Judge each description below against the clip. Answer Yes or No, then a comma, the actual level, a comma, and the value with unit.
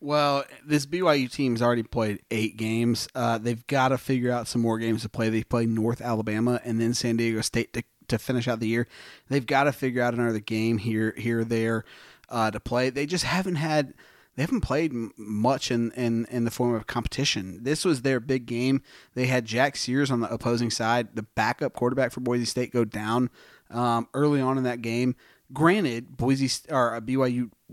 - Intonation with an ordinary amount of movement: No, narrow, 2.3 semitones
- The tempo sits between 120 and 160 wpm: No, fast, 205 wpm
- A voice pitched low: Yes, low, 120 Hz